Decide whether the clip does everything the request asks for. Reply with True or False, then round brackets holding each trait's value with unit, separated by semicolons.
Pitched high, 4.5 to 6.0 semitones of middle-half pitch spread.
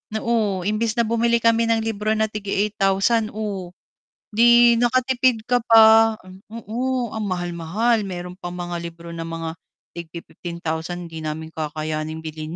True (200 Hz; 5.2 semitones)